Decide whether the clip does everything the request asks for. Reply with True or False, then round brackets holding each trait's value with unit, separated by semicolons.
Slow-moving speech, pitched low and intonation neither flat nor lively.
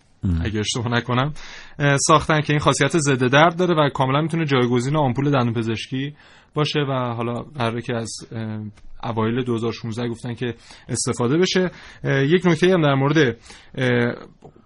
False (140 wpm; 130 Hz; 4.0 semitones)